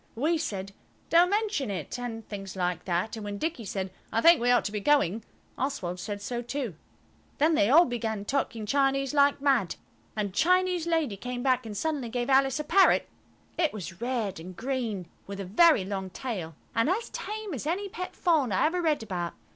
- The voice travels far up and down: Yes, wide, 7.1 semitones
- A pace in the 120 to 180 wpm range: No, average, 195 wpm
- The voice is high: Yes, high, 245 Hz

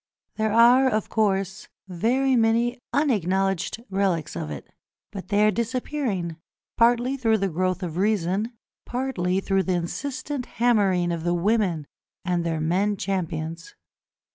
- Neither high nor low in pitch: No, high, 200 Hz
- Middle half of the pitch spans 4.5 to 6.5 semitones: Yes, average, 4.8 semitones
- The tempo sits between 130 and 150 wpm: Yes, slow, 135 wpm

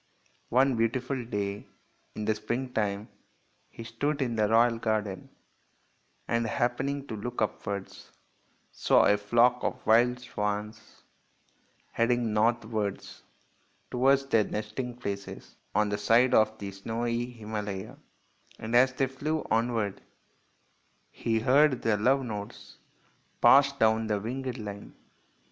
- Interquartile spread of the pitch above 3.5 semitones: No, average, 2.8 semitones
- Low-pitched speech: Yes, low, 115 Hz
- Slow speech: Yes, slow, 125 wpm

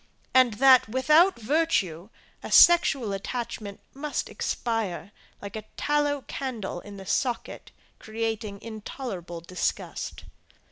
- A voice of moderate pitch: No, high, 225 Hz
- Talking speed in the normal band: No, slow, 105 wpm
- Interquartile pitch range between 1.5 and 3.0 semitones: No, average, 5.1 semitones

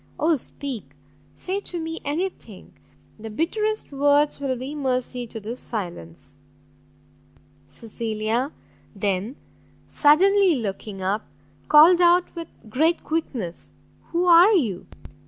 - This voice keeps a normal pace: No, slow, 115 wpm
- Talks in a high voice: Yes, very high, 275 Hz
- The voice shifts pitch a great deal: Yes, wide, 7.5 semitones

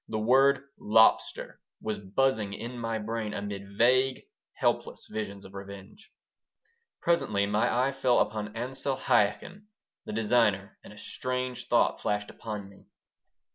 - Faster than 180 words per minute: No, slow, 135 wpm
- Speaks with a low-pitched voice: Yes, low, 110 Hz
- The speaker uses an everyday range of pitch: Yes, average, 3.7 semitones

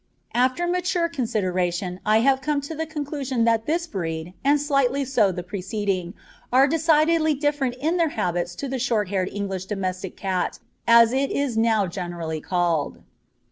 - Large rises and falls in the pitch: Yes, wide, 7.5 semitones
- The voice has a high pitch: Yes, high, 230 Hz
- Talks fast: No, average, 160 wpm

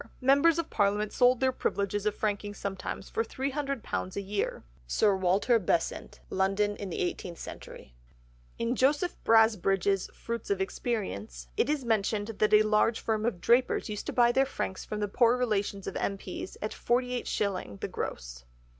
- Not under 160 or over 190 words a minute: Yes, average, 170 wpm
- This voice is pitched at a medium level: No, high, 210 Hz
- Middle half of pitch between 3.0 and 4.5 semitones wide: Yes, average, 3.7 semitones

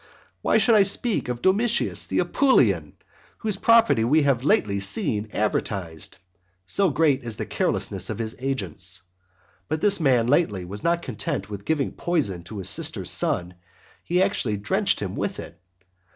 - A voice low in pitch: Yes, low, 125 Hz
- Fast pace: No, average, 160 wpm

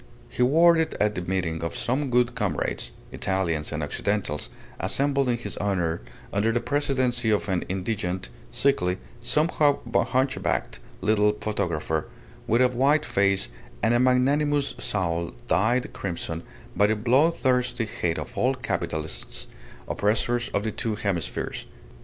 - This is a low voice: Yes, low, 110 Hz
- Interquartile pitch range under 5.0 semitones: No, wide, 5.6 semitones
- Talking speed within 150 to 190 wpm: No, slow, 135 wpm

